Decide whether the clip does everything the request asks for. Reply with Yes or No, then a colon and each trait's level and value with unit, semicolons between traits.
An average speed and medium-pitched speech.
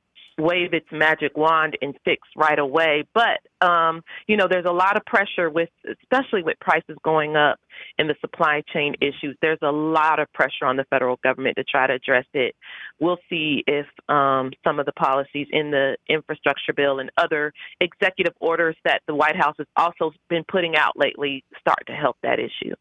Yes: average, 190 wpm; medium, 155 Hz